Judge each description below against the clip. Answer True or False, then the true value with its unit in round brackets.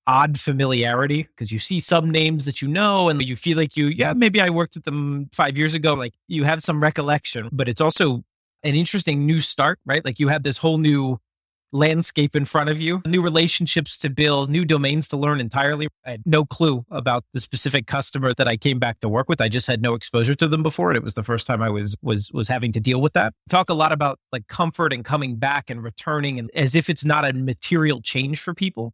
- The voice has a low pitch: False (145 Hz)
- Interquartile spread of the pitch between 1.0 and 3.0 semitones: False (3.8 semitones)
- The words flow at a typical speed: False (240 wpm)